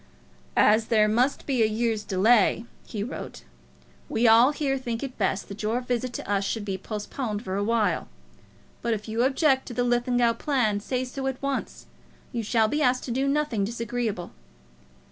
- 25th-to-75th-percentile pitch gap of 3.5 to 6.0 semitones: No, average, 3.1 semitones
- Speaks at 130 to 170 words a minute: No, average, 185 wpm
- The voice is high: Yes, high, 235 Hz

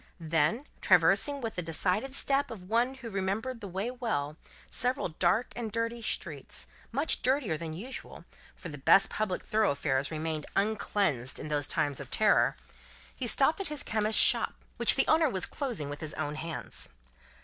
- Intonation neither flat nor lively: No, wide, 7.6 semitones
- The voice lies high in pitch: Yes, high, 205 Hz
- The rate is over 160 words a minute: Yes, average, 170 wpm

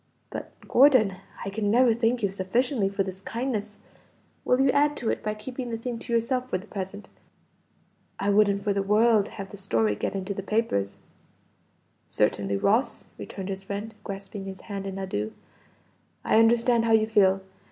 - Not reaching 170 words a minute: No, average, 175 wpm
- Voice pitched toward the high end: Yes, high, 205 Hz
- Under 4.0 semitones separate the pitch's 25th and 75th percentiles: Yes, average, 3.1 semitones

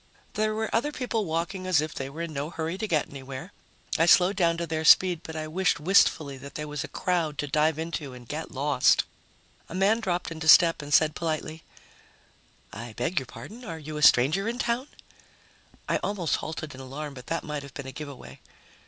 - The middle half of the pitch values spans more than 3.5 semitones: Yes, average, 3.9 semitones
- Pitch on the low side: No, medium, 160 Hz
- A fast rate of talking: Yes, fast, 210 wpm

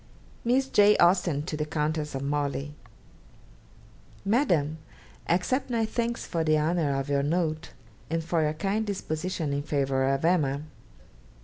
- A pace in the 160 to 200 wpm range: No, average, 140 wpm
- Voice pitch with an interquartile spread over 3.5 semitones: Yes, average, 4.2 semitones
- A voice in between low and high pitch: Yes, medium, 155 Hz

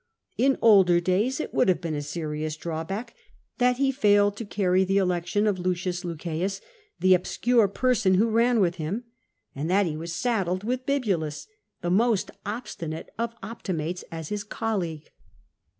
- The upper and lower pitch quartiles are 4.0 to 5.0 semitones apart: Yes, average, 4.7 semitones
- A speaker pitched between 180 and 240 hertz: Yes, high, 190 Hz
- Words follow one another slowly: No, average, 160 wpm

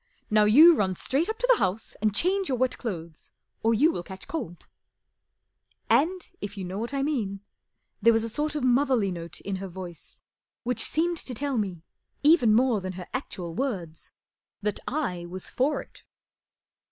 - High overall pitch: Yes, high, 225 Hz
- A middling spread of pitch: No, wide, 7.2 semitones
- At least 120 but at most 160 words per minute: No, average, 190 wpm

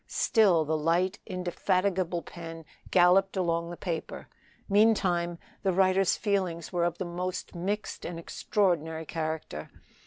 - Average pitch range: No, narrow, 2.2 semitones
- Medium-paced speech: No, slow, 125 wpm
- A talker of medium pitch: Yes, medium, 175 Hz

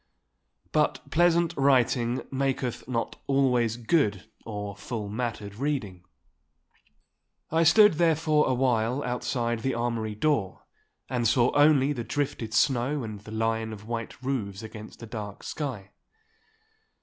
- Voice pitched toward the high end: No, low, 120 Hz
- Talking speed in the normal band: No, slow, 125 wpm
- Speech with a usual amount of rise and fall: Yes, average, 4.0 semitones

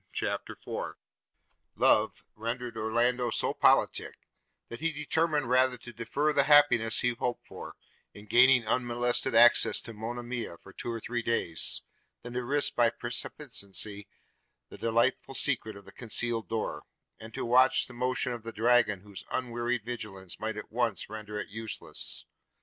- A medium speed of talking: Yes, average, 155 wpm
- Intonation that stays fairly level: Yes, narrow, 2.1 semitones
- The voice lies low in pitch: Yes, low, 120 Hz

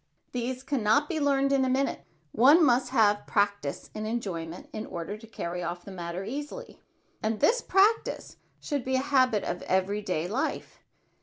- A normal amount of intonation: No, wide, 5.8 semitones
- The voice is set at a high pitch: Yes, high, 225 Hz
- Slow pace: No, average, 175 wpm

